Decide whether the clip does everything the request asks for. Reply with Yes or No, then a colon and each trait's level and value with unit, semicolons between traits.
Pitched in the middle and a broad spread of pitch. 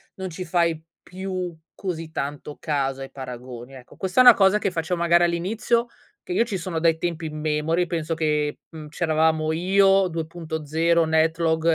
No: medium, 165 Hz; narrow, 2.6 semitones